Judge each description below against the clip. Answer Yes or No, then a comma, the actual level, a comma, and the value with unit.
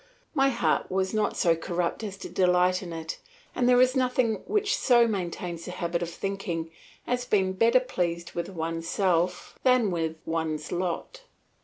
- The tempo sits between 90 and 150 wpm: No, average, 165 wpm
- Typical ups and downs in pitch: No, wide, 5.7 semitones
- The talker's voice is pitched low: No, medium, 185 Hz